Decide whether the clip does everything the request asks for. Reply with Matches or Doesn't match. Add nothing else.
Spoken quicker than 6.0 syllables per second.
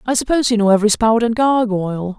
Matches